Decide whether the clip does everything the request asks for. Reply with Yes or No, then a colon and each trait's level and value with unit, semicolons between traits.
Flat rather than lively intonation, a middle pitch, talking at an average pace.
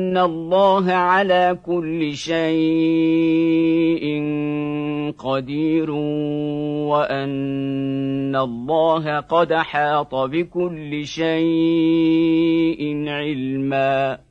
No: narrow, 1.9 semitones; medium, 155 Hz; slow, 55 wpm